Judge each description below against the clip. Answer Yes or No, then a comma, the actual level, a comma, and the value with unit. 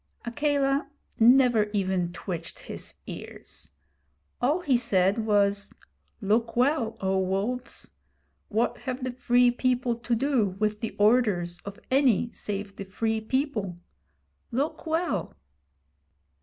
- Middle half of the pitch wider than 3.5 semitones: Yes, average, 4.1 semitones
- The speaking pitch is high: Yes, high, 230 Hz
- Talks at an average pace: No, slow, 115 wpm